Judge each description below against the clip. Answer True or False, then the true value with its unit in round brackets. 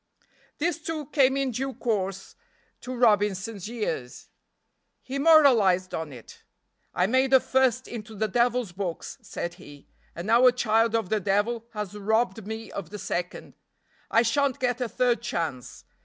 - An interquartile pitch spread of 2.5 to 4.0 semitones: False (4.5 semitones)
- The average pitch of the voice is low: False (225 Hz)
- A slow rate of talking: False (155 wpm)